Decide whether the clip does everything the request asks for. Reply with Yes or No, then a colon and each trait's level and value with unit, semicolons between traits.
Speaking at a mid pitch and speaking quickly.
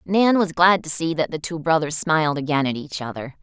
Yes: medium, 160 Hz; fast, 245 wpm